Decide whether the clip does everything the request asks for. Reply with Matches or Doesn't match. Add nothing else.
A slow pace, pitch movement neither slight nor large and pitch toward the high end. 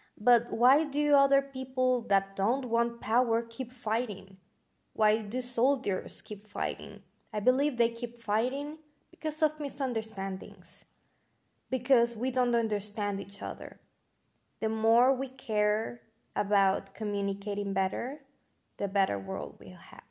Matches